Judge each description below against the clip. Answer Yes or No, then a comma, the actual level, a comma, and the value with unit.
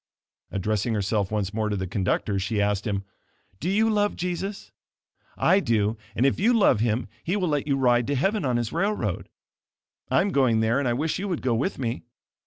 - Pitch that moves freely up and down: Yes, wide, 8.8 semitones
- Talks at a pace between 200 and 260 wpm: Yes, fast, 205 wpm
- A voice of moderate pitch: No, low, 125 Hz